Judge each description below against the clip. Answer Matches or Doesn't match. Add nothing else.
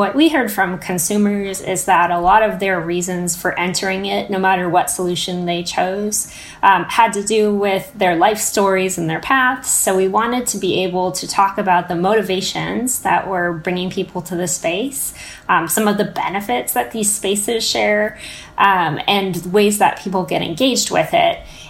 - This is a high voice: Matches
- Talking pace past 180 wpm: Matches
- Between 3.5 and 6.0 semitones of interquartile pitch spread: Doesn't match